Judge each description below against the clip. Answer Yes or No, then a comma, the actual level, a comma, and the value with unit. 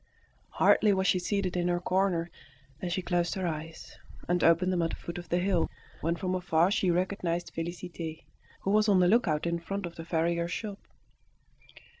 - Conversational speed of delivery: Yes, average, 190 wpm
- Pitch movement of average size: No, narrow, 1.8 semitones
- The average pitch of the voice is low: No, medium, 175 Hz